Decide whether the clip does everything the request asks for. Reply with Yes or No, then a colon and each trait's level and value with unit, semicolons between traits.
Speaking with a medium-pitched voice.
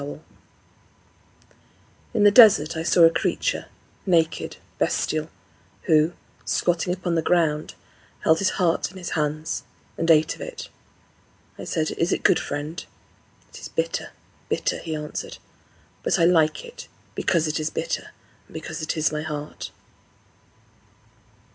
Yes: medium, 165 Hz